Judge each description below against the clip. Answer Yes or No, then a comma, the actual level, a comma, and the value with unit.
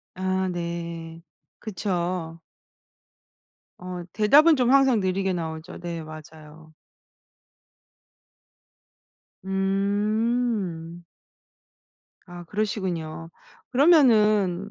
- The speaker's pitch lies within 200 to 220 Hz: No, medium, 185 Hz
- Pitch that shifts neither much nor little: Yes, average, 4.0 semitones